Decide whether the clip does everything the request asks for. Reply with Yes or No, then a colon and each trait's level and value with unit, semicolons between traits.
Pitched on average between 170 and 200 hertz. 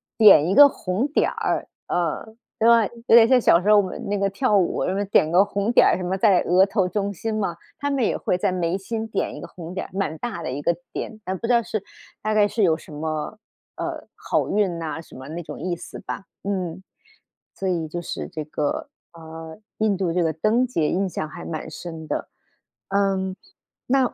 Yes: high, 190 Hz